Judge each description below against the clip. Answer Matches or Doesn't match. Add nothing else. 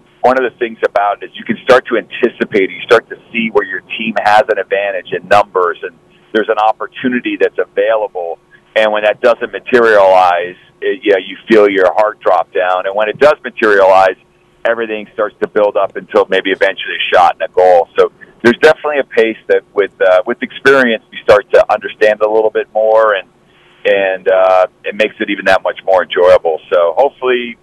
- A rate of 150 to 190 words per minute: Doesn't match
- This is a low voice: Matches